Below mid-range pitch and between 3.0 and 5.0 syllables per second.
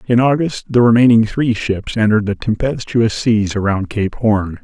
Yes: low, 110 Hz; 4.7 syllables/s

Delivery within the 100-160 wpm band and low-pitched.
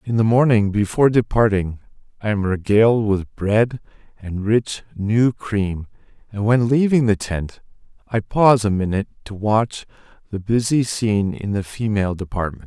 Yes: average, 150 wpm; low, 105 Hz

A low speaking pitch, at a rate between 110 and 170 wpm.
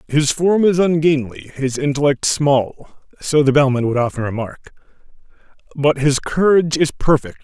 No: medium, 145 Hz; slow, 135 wpm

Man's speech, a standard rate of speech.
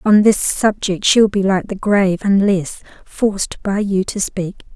No: female; average, 190 wpm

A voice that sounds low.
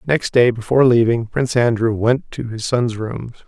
Yes: low, 120 Hz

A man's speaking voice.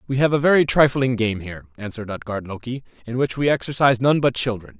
Yes: male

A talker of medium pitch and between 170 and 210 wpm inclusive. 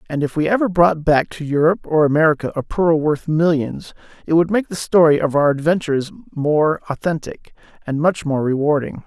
Yes: medium, 155 Hz; average, 180 wpm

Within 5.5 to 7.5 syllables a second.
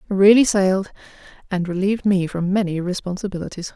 Yes: 6.1 syllables/s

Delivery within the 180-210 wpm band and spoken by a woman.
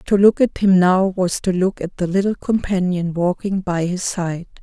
Yes: fast, 205 wpm; female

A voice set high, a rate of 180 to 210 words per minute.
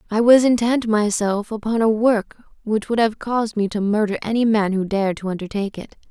Yes: high, 215 Hz; fast, 205 wpm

